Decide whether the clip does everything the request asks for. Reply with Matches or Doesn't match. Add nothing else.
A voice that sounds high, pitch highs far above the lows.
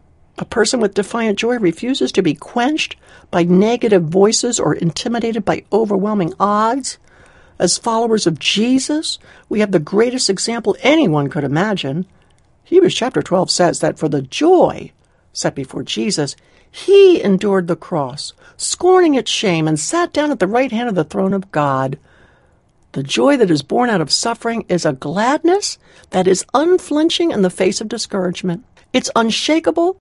Matches